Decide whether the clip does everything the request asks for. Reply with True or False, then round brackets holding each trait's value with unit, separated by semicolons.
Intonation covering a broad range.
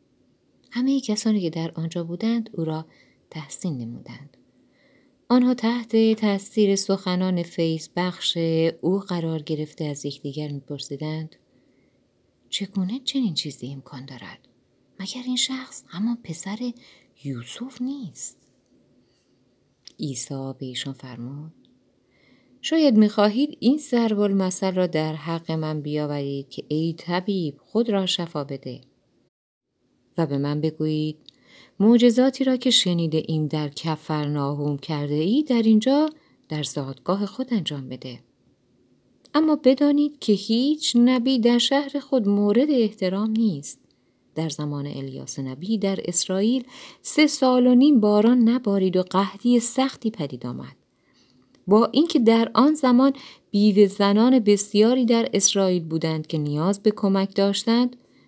True (7.7 semitones)